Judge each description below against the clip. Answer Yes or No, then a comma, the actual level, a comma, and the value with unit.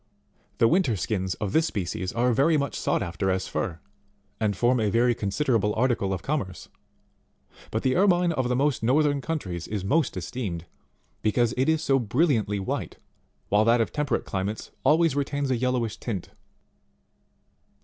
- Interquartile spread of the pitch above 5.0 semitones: Yes, wide, 5.5 semitones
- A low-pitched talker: Yes, low, 120 Hz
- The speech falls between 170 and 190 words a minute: No, average, 160 wpm